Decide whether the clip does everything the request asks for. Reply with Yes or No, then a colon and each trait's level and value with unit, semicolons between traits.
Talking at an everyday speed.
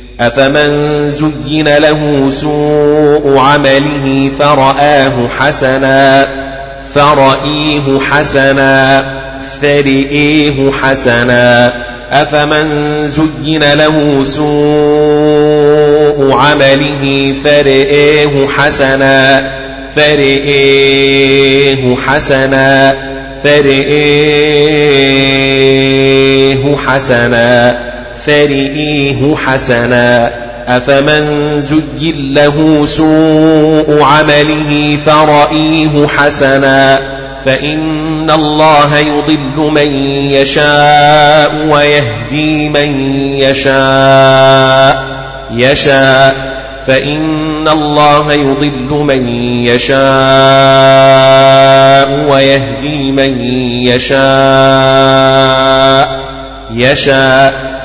No: slow, 50 wpm